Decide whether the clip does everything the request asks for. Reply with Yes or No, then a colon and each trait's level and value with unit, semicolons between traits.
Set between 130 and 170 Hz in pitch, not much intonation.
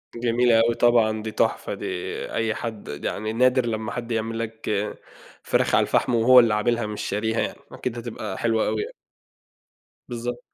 No: low, 115 Hz; narrow, 1.5 semitones